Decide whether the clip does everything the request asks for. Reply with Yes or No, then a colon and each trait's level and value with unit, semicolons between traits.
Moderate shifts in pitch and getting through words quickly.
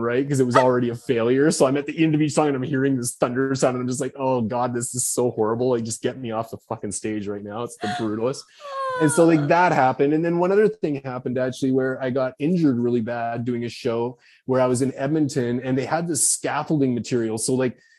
Yes: average, 3.3 semitones; fast, 260 wpm